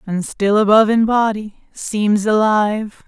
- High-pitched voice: Yes, high, 210 Hz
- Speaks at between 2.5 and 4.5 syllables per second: Yes, 4.2 syllables/s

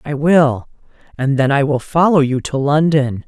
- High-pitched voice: No, medium, 145 Hz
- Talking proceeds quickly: No, average, 165 wpm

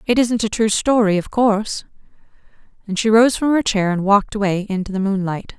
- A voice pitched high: Yes, high, 210 Hz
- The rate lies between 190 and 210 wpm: Yes, fast, 205 wpm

